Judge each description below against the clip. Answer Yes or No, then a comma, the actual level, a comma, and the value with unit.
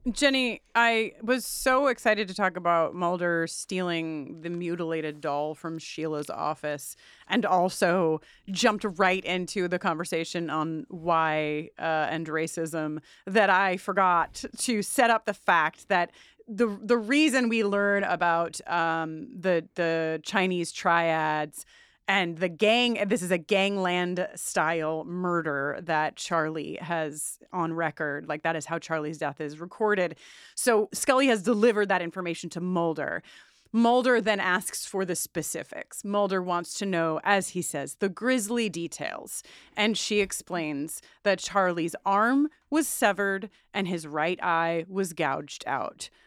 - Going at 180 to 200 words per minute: No, average, 140 wpm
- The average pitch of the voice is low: No, medium, 180 Hz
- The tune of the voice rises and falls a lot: No, average, 4.2 semitones